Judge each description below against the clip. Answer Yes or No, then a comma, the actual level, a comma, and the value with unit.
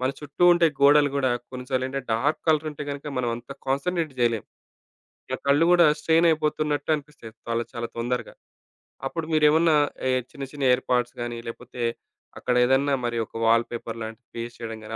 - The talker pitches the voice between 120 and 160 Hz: Yes, low, 135 Hz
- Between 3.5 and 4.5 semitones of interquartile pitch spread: Yes, average, 4.0 semitones